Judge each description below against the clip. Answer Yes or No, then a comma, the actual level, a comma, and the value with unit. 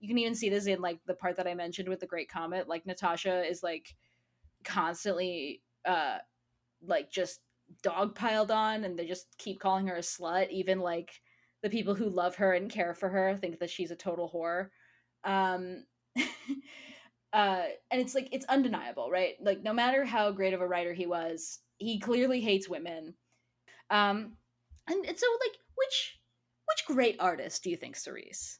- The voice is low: No, medium, 185 Hz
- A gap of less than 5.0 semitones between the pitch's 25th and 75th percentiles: Yes, average, 4.1 semitones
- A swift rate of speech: No, average, 185 wpm